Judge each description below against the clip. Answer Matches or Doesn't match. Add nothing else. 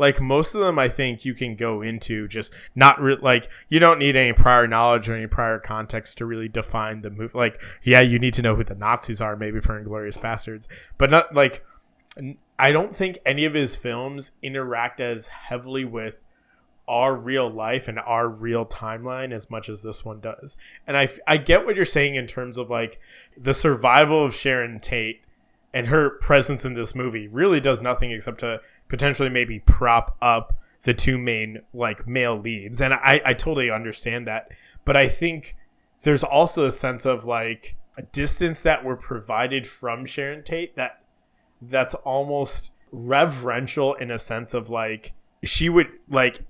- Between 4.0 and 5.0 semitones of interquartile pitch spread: Doesn't match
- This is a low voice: Matches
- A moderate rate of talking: Matches